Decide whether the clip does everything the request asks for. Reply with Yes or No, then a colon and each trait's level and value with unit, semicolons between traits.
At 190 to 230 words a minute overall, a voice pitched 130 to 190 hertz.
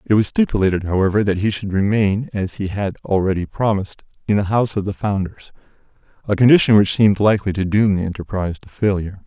No: average, 195 wpm; low, 100 Hz